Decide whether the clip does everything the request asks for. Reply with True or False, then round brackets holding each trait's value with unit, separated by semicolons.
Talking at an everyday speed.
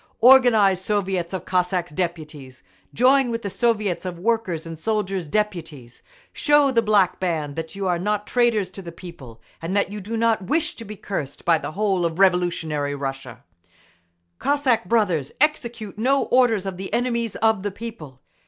True (170 wpm)